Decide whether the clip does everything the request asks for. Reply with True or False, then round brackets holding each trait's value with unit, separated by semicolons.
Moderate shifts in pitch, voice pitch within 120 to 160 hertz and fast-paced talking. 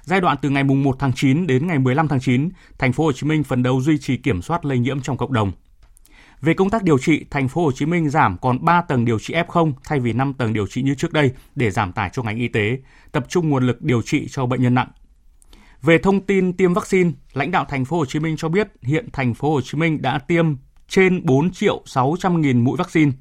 True (4.5 semitones; 140 Hz; 255 wpm)